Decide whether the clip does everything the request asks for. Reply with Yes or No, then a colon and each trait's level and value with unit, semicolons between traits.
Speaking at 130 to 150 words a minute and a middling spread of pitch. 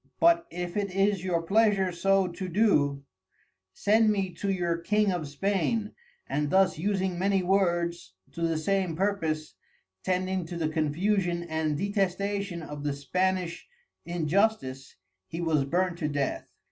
Yes: average, 145 wpm; average, 3.4 semitones